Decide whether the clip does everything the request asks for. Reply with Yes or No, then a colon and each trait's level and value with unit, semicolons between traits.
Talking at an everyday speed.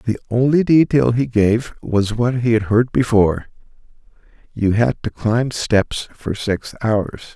Yes: average, 155 wpm